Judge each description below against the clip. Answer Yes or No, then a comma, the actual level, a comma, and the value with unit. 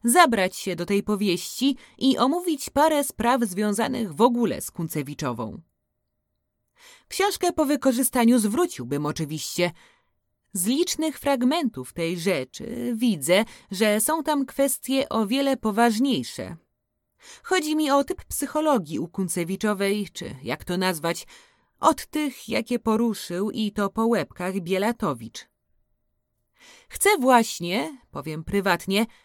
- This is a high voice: Yes, high, 225 Hz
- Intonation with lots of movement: Yes, wide, 7.0 semitones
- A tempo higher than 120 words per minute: No, average, 115 wpm